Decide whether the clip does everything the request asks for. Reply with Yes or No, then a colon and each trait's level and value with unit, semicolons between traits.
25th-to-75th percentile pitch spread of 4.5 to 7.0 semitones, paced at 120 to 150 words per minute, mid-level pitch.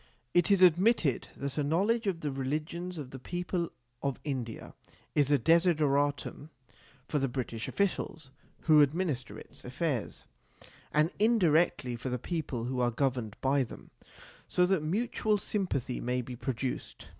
Yes: average, 5.2 semitones; average, 145 wpm; medium, 150 Hz